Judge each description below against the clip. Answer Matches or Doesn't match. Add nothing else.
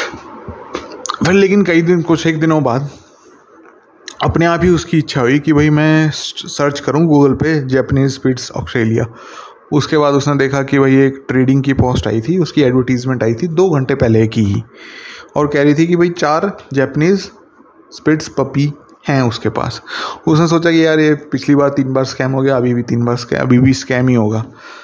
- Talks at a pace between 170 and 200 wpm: Matches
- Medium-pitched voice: Matches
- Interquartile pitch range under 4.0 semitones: Matches